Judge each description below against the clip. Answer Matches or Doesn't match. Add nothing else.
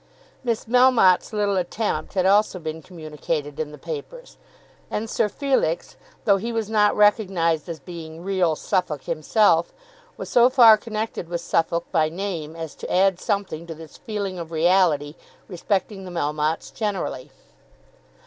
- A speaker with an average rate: Matches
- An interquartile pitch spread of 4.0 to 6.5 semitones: Matches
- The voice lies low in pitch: Doesn't match